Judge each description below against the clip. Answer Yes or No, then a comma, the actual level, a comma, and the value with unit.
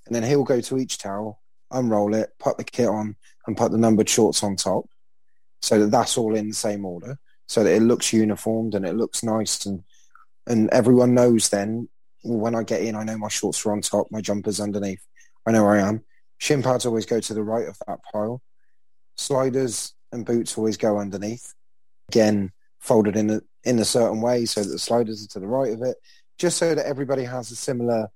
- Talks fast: Yes, fast, 215 wpm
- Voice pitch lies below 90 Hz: No, low, 110 Hz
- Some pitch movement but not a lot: No, narrow, 2.3 semitones